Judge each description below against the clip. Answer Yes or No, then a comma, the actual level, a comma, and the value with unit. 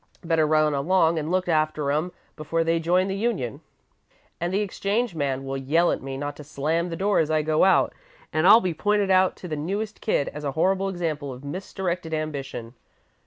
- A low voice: No, medium, 165 Hz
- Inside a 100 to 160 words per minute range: No, fast, 205 wpm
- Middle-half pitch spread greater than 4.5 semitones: No, average, 3.9 semitones